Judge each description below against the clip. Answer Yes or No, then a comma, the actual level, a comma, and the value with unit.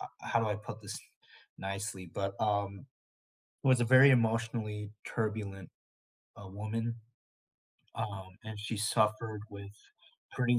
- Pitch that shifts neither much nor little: No, narrow, 2.2 semitones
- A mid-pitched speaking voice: No, low, 105 Hz